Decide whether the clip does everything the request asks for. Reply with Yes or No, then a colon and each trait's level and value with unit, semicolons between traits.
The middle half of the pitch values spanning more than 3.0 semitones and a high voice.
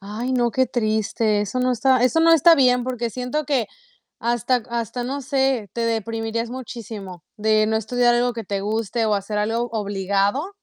No: average, 2.7 semitones; high, 235 Hz